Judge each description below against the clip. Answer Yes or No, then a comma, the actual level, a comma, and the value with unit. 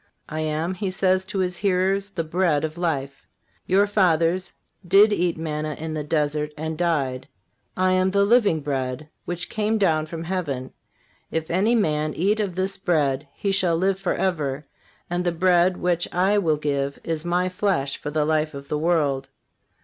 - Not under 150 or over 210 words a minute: Yes, average, 175 wpm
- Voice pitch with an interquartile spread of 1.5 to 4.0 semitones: Yes, average, 3.6 semitones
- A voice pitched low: No, medium, 170 Hz